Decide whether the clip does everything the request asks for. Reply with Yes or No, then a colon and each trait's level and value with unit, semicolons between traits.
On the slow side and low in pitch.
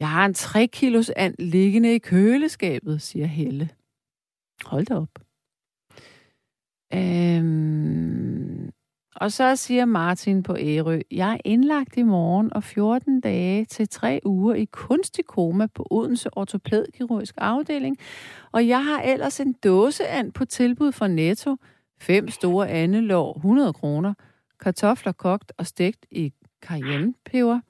No: slow, 130 wpm; high, 205 Hz